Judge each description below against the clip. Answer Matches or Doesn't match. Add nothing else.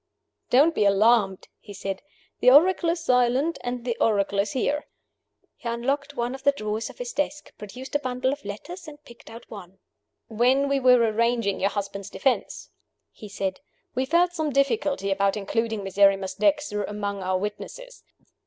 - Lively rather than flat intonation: Matches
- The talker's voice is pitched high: Matches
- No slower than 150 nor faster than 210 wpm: Matches